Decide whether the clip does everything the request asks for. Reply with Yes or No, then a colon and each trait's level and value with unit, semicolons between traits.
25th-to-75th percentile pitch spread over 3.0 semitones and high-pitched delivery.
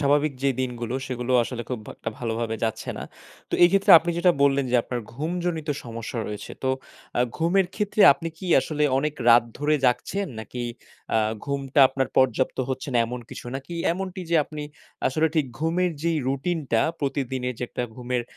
No: average, 4.9 semitones; medium, 140 Hz